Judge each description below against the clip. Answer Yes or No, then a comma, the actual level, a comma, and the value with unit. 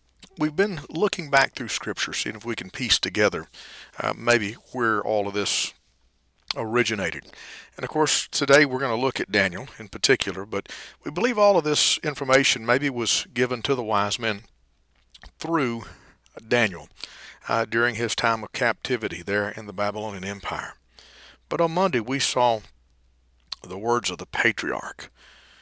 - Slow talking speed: No, average, 160 wpm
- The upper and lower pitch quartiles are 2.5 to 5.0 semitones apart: No, wide, 5.5 semitones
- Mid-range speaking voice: No, low, 115 Hz